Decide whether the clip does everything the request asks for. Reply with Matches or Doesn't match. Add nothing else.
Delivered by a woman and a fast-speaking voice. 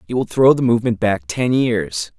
Doesn't match